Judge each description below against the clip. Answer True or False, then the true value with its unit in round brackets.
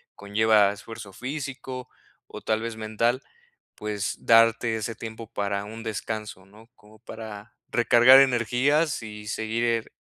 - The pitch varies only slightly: True (1.9 semitones)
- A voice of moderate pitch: False (110 Hz)